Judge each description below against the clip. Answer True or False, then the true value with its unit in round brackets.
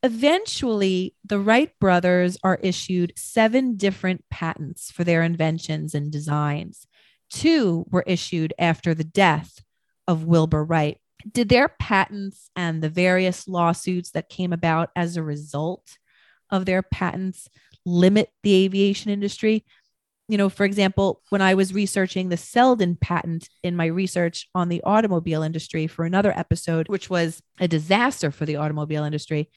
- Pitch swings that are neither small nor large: True (3.3 semitones)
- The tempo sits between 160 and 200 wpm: False (145 wpm)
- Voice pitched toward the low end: False (180 Hz)